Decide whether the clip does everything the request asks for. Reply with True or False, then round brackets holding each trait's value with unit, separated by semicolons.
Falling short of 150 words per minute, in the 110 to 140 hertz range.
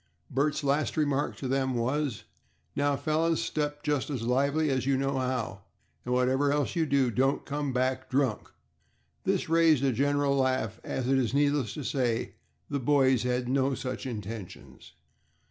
False (165 wpm; 135 Hz)